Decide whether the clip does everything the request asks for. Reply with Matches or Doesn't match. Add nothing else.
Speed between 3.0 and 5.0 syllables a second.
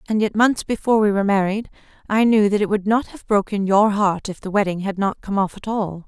Doesn't match